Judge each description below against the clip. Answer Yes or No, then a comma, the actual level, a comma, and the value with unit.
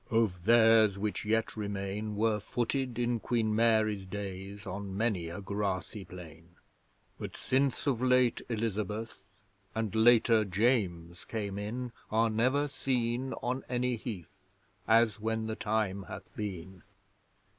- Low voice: Yes, low, 110 Hz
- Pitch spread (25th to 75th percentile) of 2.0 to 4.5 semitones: Yes, average, 2.9 semitones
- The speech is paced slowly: Yes, slow, 130 wpm